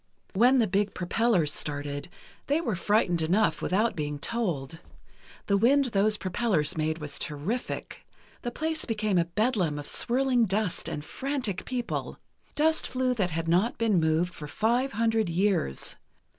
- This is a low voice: No, high, 205 Hz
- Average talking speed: Yes, average, 150 wpm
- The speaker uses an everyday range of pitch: No, wide, 6.3 semitones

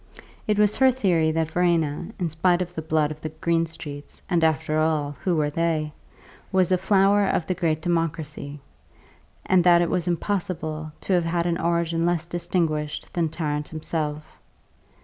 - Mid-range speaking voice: Yes, medium, 165 Hz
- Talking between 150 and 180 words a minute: Yes, average, 170 wpm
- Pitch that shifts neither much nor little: No, narrow, 2.2 semitones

